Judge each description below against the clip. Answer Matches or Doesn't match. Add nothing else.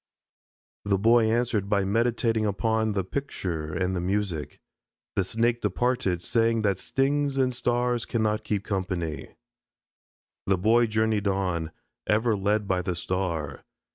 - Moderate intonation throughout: Matches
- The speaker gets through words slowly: Matches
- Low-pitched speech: Matches